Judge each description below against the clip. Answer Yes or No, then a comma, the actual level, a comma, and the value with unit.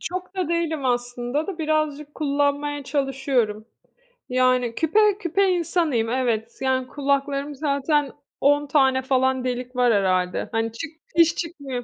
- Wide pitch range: No, average, 3.6 semitones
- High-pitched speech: Yes, very high, 275 Hz